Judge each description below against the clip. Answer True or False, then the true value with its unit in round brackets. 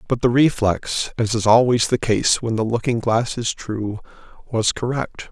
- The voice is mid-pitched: False (115 Hz)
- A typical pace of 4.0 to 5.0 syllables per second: True (4.4 syllables/s)